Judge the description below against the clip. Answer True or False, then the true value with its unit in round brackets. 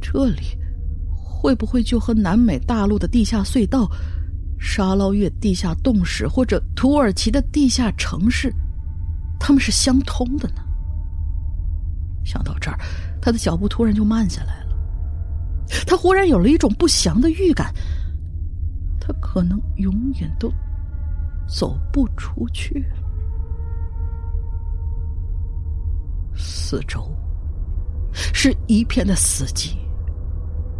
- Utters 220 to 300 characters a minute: False (170 characters per minute)